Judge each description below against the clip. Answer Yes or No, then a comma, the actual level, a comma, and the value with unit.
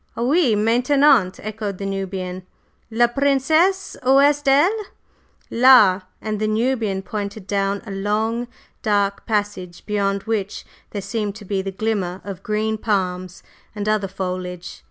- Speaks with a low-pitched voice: No, high, 210 Hz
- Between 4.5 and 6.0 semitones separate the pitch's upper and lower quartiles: No, average, 3.4 semitones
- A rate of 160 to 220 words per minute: No, slow, 135 wpm